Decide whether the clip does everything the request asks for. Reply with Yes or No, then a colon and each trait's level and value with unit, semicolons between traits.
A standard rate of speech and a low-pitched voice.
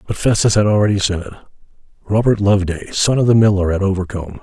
Yes: average, 175 wpm; low, 100 Hz